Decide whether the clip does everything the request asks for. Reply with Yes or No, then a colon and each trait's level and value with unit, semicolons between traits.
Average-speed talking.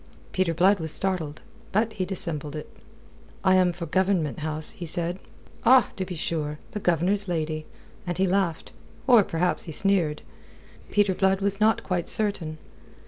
Yes: average, 160 wpm